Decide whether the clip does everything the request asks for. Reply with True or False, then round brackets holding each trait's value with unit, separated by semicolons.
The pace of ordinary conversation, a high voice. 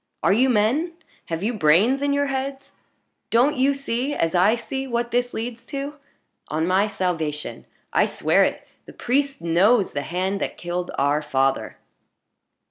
True (160 wpm; 225 Hz)